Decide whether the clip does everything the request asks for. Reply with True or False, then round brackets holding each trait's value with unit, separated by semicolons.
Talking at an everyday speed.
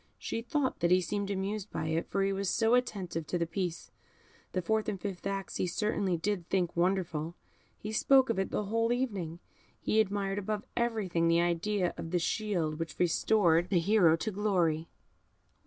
True (190 wpm)